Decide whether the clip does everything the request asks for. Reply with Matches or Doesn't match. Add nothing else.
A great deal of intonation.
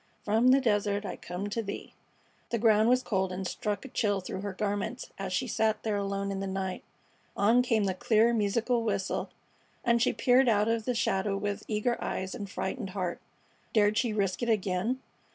Doesn't match